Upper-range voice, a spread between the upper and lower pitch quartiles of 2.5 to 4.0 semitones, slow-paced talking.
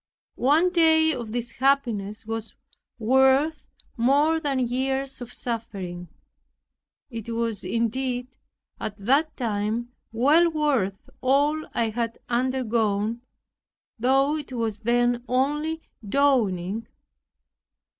Yes: high, 245 Hz; average, 3.7 semitones; slow, 100 wpm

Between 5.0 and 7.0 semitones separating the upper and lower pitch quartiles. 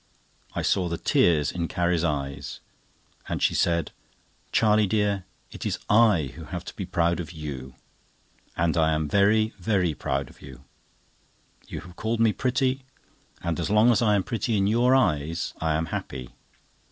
Yes: wide, 5.4 semitones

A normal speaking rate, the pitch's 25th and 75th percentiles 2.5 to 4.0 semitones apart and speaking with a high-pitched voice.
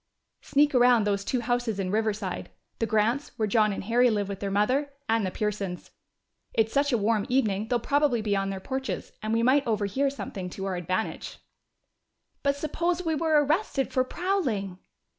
No: average, 180 wpm; average, 5.3 semitones; high, 225 Hz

